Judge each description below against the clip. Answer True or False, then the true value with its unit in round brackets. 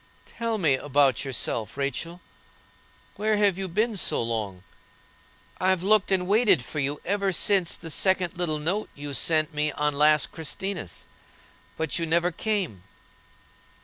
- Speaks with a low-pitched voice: False (165 Hz)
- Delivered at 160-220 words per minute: False (145 wpm)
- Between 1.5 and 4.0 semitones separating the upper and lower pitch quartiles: False (5.0 semitones)